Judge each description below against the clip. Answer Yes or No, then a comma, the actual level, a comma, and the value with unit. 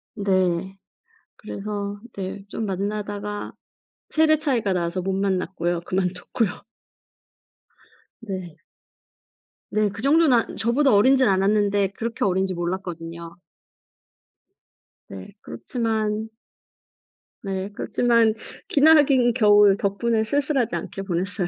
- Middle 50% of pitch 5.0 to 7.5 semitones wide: No, average, 3.3 semitones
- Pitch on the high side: Yes, high, 205 Hz